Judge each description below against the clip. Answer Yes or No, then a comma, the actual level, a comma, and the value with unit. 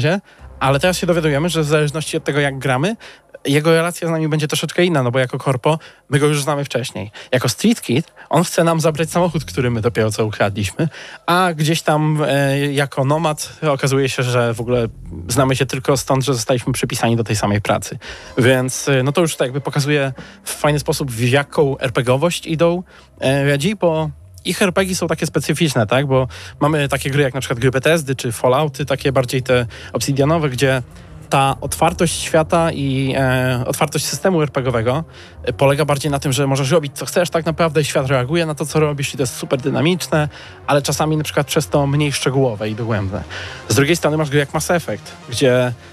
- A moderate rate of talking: No, fast, 195 wpm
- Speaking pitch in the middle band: Yes, medium, 145 Hz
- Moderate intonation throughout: Yes, average, 3.4 semitones